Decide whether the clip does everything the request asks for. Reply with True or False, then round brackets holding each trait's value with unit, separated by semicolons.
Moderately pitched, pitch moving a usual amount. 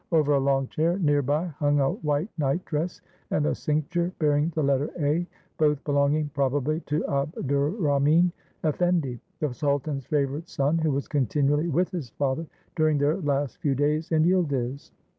False (150 Hz; 2.2 semitones)